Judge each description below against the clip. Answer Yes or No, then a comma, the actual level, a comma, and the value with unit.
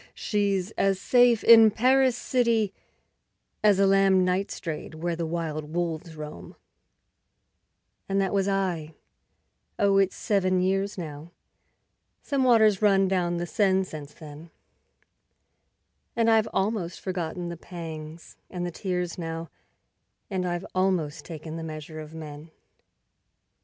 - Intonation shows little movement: No, average, 3.4 semitones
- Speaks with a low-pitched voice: No, medium, 180 Hz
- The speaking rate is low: Yes, slow, 130 wpm